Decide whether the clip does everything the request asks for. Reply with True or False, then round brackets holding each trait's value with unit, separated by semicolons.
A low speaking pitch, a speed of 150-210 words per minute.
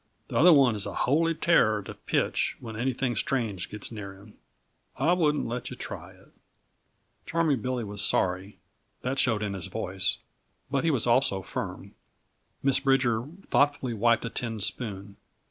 True (120 Hz; 165 wpm)